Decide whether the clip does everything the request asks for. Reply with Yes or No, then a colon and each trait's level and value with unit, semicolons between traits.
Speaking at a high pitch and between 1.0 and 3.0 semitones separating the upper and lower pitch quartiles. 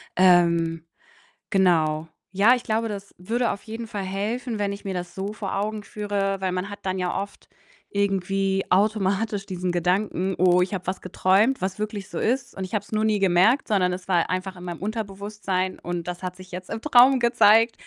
Yes: high, 195 Hz; narrow, 2.6 semitones